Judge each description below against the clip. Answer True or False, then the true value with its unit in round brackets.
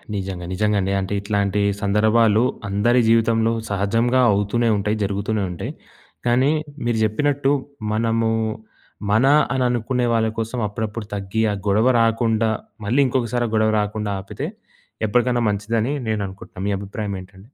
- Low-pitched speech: True (110 Hz)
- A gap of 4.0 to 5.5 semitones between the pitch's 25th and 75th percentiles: False (2.5 semitones)